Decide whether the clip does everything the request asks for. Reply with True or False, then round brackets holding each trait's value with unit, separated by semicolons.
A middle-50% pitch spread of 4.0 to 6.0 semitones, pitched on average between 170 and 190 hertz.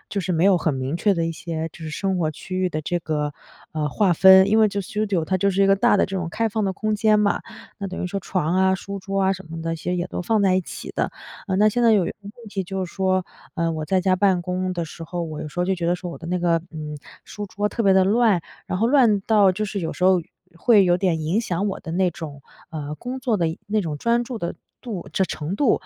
False (3.2 semitones; 185 Hz)